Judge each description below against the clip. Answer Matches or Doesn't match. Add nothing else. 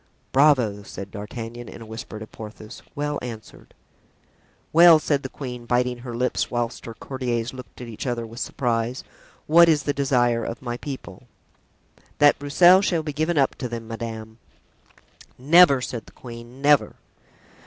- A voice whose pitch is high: Doesn't match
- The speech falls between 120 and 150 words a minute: Doesn't match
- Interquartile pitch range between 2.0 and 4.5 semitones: Matches